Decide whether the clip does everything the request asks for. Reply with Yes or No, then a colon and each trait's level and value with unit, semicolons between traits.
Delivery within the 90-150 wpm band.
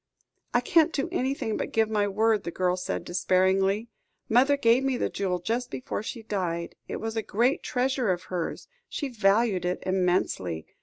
No: average, 175 wpm